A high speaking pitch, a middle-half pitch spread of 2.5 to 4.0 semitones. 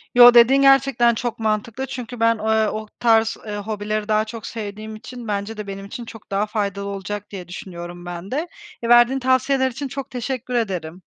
Yes: high, 220 Hz; average, 3.1 semitones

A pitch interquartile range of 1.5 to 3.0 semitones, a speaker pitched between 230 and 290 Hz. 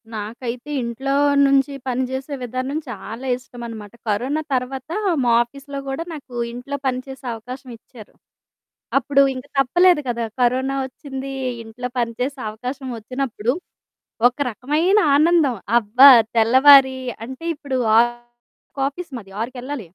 Yes: narrow, 2.5 semitones; very high, 255 Hz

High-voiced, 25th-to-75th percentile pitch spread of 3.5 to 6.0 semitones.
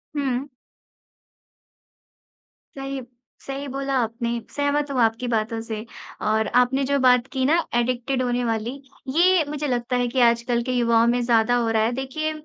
No: very high, 250 Hz; average, 2.7 semitones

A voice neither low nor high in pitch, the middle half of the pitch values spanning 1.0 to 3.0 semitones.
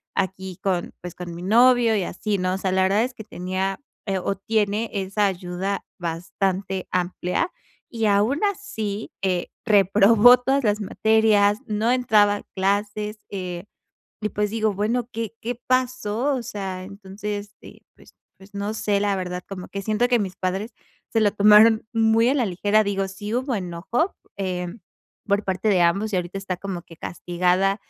No: high, 205 Hz; average, 2.7 semitones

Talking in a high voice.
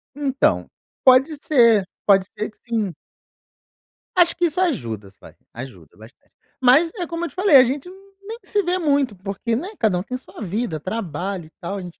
Yes: high, 235 Hz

